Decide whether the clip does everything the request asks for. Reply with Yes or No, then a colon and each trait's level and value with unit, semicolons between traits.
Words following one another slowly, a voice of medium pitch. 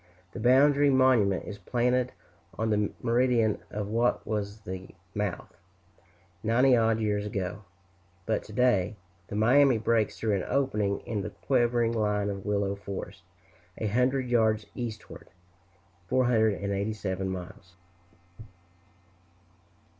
No: slow, 115 wpm; low, 110 Hz